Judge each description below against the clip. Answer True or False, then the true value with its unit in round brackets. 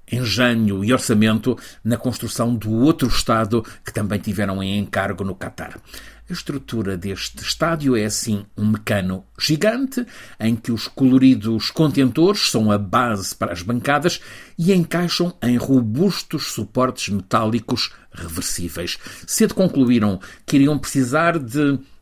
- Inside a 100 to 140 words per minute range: True (130 wpm)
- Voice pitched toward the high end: False (120 Hz)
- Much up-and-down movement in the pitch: False (5.0 semitones)